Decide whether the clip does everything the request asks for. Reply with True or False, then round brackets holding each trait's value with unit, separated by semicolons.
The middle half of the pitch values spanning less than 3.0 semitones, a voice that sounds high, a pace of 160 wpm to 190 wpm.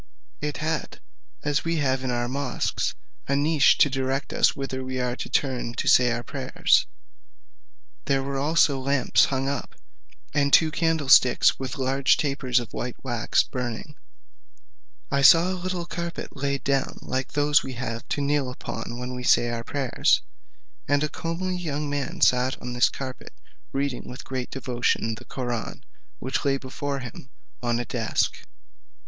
False (2.4 semitones; 135 Hz; 165 wpm)